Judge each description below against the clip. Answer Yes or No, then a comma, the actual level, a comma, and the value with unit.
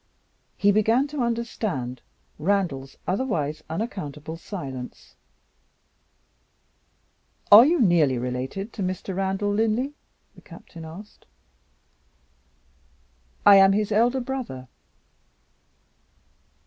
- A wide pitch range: Yes, wide, 6.6 semitones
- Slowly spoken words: Yes, slow, 85 wpm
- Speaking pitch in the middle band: No, high, 195 Hz